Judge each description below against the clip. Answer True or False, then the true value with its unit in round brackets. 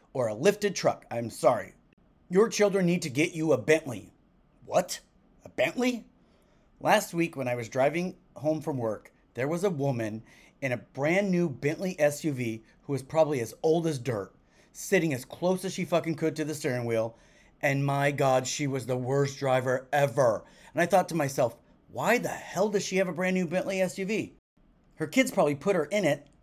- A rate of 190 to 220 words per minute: True (195 wpm)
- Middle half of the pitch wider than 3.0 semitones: True (5.1 semitones)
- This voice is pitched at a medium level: True (155 Hz)